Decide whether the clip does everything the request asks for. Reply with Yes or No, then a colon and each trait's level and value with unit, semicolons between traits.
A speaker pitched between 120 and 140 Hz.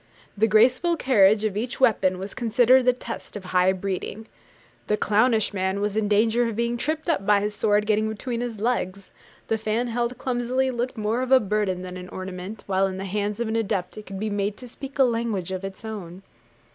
No: high, 215 Hz